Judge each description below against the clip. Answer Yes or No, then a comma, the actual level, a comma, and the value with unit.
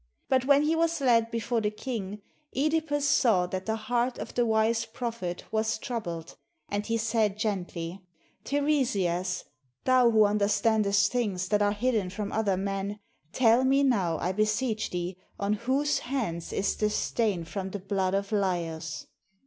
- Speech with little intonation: No, average, 3.9 semitones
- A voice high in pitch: Yes, high, 215 Hz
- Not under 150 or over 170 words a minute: Yes, average, 160 wpm